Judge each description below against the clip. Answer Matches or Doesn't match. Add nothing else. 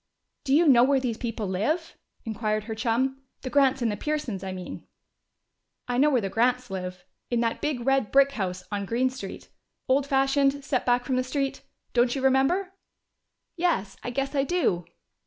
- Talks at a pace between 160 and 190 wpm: Matches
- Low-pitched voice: Doesn't match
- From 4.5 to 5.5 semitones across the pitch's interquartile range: Doesn't match